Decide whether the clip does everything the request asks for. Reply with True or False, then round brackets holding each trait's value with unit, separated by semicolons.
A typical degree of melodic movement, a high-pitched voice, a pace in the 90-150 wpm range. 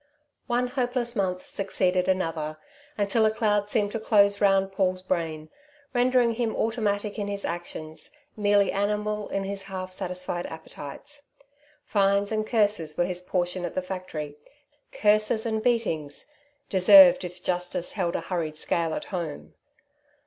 True (3.3 semitones; 195 Hz; 140 wpm)